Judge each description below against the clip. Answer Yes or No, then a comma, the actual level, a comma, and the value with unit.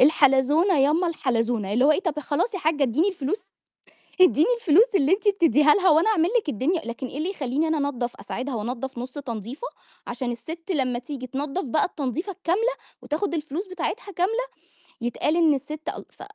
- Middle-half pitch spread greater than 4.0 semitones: Yes, wide, 5.4 semitones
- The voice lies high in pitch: Yes, very high, 300 Hz